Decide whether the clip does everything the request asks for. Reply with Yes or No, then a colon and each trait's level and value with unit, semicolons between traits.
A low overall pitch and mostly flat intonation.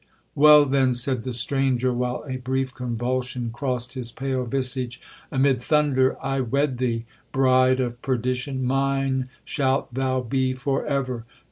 Yes: low, 130 Hz; narrow, 1.4 semitones